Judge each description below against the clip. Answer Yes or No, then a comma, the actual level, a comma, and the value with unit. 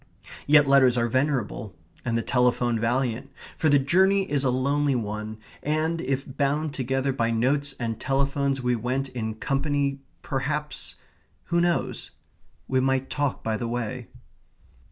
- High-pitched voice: No, low, 135 Hz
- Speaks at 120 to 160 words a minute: Yes, average, 145 wpm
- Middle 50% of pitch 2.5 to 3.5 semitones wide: Yes, average, 2.9 semitones